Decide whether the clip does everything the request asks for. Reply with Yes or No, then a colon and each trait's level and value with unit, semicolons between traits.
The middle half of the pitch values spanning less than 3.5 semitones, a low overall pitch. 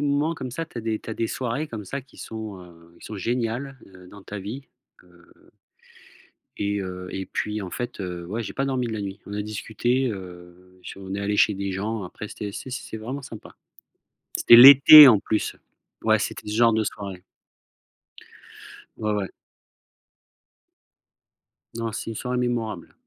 No: average, 3.8 semitones; low, 110 Hz